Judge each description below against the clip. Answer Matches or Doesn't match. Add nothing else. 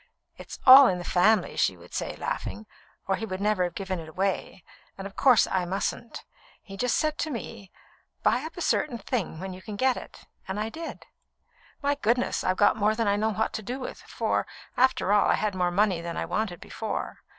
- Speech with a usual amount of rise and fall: Matches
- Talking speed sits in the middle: Doesn't match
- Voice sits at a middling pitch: Doesn't match